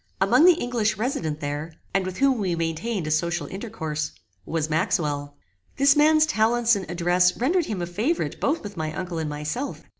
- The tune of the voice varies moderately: No, wide, 7.1 semitones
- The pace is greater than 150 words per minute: Yes, average, 180 wpm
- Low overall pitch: No, medium, 185 Hz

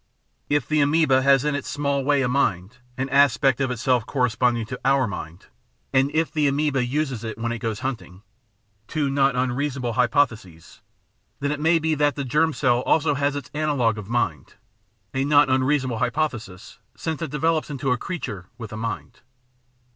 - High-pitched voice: No, low, 130 Hz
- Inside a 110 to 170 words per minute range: No, average, 185 wpm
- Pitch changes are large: No, average, 3.9 semitones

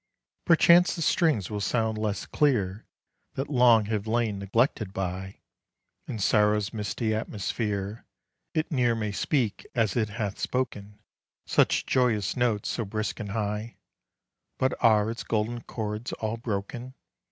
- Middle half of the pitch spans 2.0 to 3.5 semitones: Yes, narrow, 2.6 semitones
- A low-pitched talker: Yes, low, 110 Hz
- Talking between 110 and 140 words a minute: Yes, slow, 135 wpm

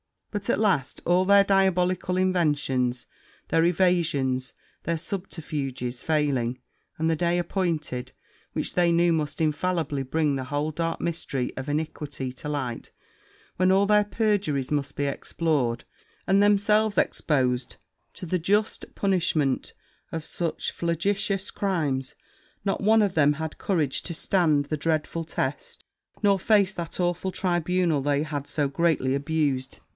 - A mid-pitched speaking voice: Yes, medium, 165 Hz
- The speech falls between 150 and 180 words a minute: No, average, 140 wpm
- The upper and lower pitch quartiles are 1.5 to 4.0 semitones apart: No, average, 4.5 semitones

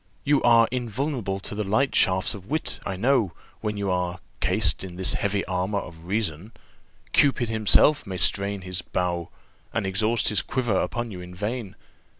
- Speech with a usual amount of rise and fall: Yes, average, 3.9 semitones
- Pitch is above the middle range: No, low, 100 Hz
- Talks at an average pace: Yes, average, 170 wpm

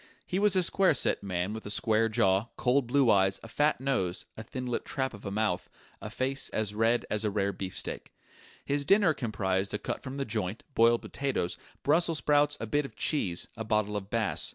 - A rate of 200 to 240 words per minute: Yes, fast, 205 wpm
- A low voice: Yes, low, 115 Hz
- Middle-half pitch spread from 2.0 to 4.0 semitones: No, average, 5.1 semitones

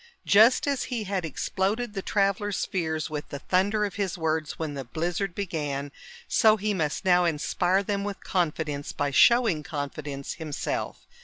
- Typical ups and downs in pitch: Yes, average, 4.8 semitones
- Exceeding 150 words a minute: Yes, average, 160 wpm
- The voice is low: No, medium, 180 Hz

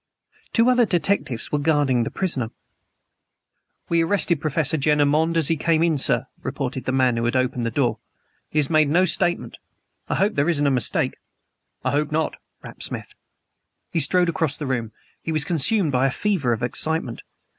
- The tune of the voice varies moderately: Yes, average, 4.1 semitones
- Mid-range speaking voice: Yes, medium, 150 Hz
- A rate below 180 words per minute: No, average, 185 wpm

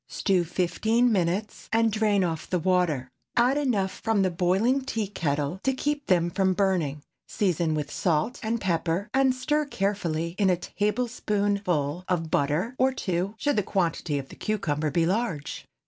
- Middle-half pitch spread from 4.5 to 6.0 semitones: Yes, average, 4.9 semitones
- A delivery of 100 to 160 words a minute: Yes, average, 155 wpm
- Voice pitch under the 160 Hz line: No, high, 190 Hz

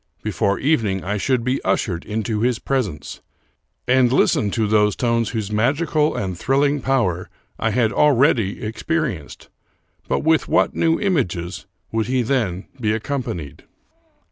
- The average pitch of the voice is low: Yes, low, 115 Hz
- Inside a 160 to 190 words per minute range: No, average, 140 wpm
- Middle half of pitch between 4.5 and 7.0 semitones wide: Yes, average, 4.9 semitones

